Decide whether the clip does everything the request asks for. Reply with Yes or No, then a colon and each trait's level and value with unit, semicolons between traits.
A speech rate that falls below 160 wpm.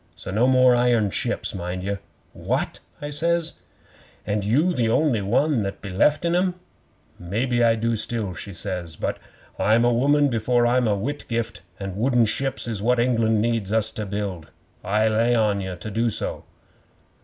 No: average, 175 wpm